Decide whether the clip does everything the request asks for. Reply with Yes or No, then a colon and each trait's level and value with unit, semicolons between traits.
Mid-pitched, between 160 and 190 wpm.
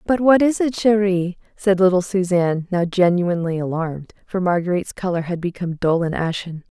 Yes: medium, 180 Hz; average, 170 wpm